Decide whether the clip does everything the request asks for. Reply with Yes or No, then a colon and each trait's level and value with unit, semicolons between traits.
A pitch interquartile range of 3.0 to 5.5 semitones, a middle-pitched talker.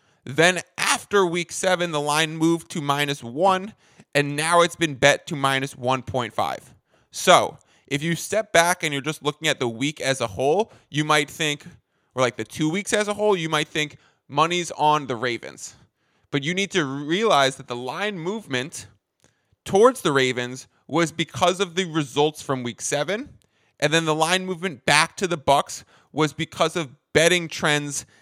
Yes: average, 4.1 semitones; medium, 150 Hz